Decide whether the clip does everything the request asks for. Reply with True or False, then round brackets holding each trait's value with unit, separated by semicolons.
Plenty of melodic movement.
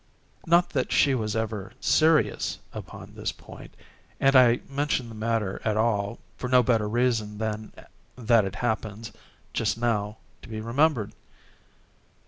False (2.8 semitones)